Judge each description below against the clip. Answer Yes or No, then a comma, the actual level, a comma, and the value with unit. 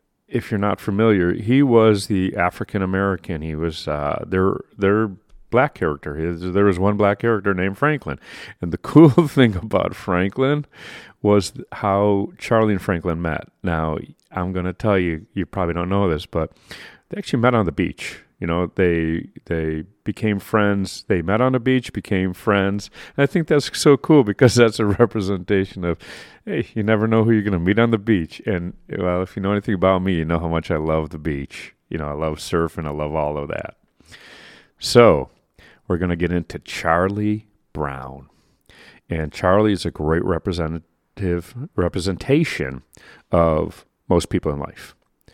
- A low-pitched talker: Yes, very low, 95 Hz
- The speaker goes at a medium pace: Yes, average, 180 wpm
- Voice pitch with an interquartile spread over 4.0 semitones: Yes, average, 4.4 semitones